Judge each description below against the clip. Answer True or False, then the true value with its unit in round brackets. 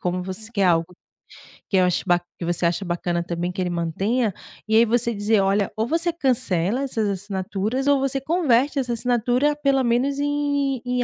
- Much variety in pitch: True (6.5 semitones)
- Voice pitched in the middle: False (225 Hz)